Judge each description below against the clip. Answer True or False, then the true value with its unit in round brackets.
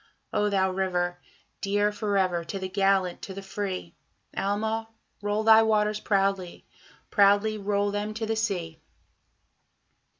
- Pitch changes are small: True (1.8 semitones)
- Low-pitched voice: False (200 Hz)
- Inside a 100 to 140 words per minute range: True (135 wpm)